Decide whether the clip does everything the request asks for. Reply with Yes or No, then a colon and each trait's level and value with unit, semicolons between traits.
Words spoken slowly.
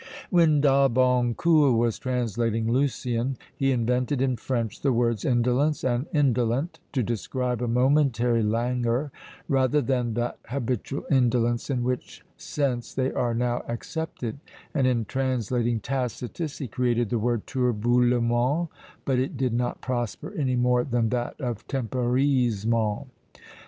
Yes: slow, 130 wpm